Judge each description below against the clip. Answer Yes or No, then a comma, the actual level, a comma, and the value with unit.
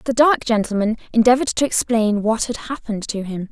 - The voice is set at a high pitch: Yes, high, 230 Hz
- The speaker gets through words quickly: No, average, 190 wpm